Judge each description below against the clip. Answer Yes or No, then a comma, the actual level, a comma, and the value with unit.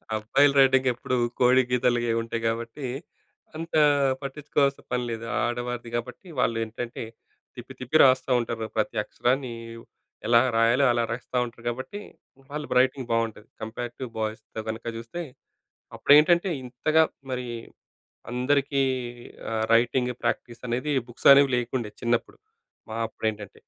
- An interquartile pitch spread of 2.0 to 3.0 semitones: Yes, narrow, 2.4 semitones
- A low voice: Yes, low, 125 Hz